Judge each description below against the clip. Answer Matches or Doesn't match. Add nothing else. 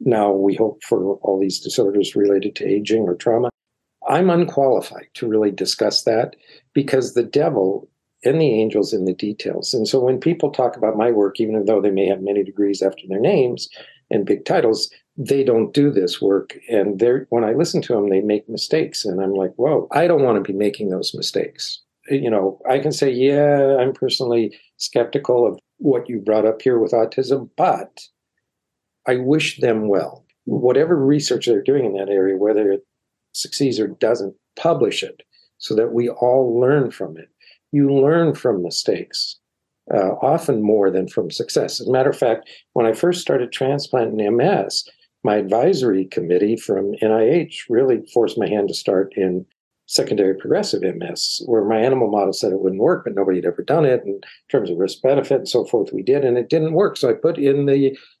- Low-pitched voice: Matches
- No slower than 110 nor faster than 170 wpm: Doesn't match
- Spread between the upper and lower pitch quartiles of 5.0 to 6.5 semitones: Matches